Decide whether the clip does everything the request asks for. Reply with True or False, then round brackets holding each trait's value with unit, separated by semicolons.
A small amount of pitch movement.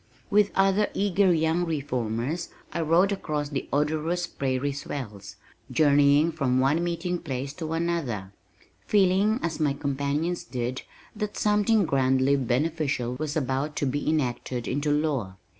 False (4.3 semitones)